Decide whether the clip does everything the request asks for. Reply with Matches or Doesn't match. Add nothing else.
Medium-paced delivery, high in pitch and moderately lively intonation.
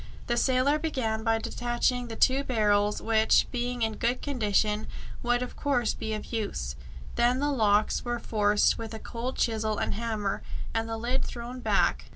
Doesn't match